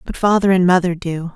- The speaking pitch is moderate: Yes, medium, 180 Hz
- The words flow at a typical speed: No, fast, 220 wpm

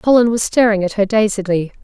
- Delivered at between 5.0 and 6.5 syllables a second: Yes, 5.9 syllables/s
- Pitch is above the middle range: Yes, high, 210 Hz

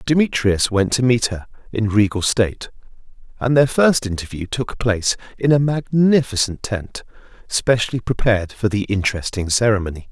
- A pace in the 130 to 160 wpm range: Yes, average, 140 wpm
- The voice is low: Yes, low, 110 Hz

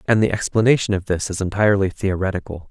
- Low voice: Yes, very low, 95 Hz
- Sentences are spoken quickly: No, average, 180 wpm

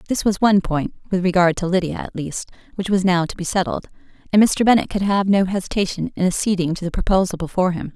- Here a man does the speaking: No, female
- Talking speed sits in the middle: No, fast, 225 wpm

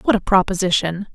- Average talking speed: Yes, average, 155 wpm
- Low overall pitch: No, high, 190 Hz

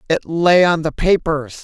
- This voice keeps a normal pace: Yes, average, 185 wpm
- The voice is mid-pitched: Yes, medium, 165 Hz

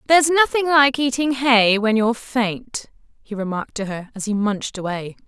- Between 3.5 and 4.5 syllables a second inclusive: No, 5.2 syllables/s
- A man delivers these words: No, female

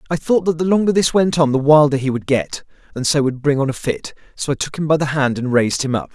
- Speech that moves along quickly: Yes, fast, 305 wpm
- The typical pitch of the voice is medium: Yes, medium, 145 Hz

